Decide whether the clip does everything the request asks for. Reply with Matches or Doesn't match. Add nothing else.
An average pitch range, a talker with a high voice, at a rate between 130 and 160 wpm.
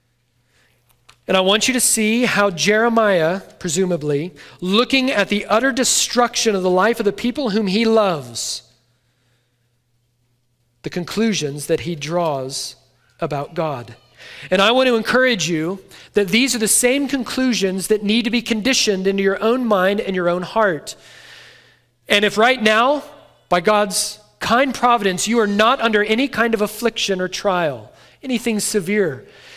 Doesn't match